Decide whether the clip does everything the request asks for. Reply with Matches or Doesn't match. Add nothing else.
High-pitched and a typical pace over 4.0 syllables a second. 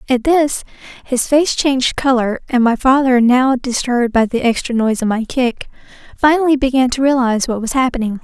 Matches